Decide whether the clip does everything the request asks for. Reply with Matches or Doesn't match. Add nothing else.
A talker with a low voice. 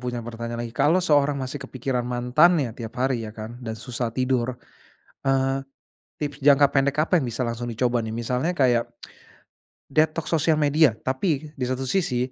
Matches